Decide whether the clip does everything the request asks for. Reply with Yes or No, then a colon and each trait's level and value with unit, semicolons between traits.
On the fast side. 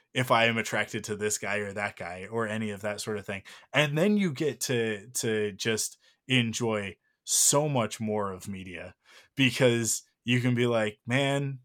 No: average, 185 wpm